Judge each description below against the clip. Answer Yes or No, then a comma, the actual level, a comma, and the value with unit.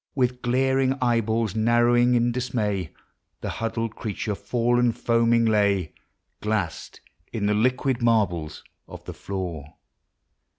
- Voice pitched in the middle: No, low, 115 Hz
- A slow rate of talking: Yes, slow, 115 wpm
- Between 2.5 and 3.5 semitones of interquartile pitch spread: Yes, average, 2.8 semitones